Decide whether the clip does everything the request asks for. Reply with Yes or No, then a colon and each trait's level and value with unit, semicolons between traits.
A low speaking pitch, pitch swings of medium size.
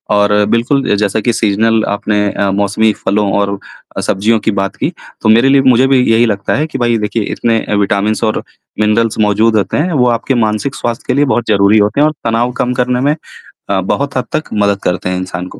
Yes: low, 110 Hz; average, 3.4 semitones